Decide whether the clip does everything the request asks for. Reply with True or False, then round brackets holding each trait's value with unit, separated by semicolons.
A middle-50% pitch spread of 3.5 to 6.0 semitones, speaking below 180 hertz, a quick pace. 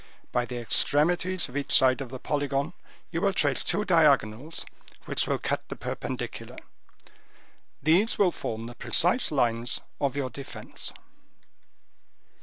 False (5.3 semitones; 140 Hz; 135 wpm)